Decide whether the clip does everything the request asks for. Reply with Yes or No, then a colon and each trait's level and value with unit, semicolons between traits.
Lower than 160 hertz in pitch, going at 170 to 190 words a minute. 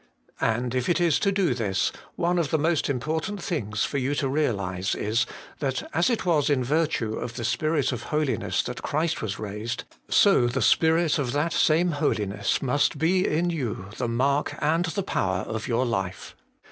Yes: medium, 140 Hz; average, 185 wpm